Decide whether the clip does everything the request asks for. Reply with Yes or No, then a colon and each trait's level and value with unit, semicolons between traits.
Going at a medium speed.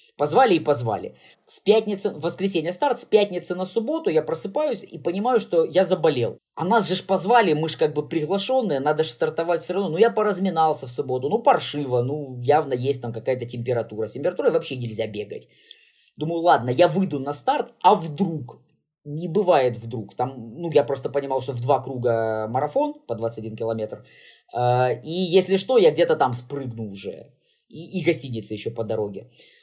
No: fast, 180 wpm